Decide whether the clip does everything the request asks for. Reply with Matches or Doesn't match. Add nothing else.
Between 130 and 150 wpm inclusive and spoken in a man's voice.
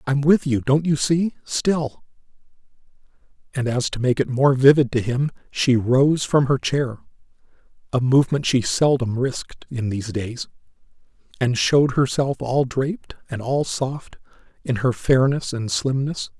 Matches